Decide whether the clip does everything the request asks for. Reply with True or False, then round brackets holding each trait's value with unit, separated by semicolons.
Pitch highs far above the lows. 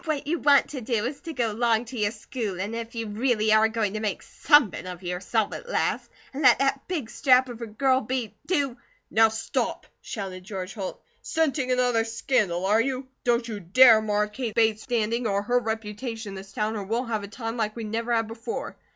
False (3.1 semitones)